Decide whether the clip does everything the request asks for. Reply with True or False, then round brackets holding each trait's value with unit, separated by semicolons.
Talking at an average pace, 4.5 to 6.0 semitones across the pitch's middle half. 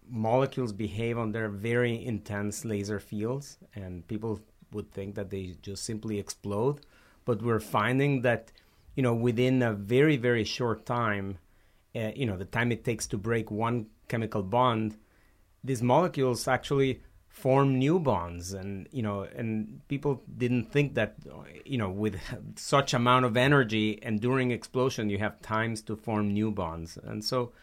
False (160 wpm; 3.3 semitones)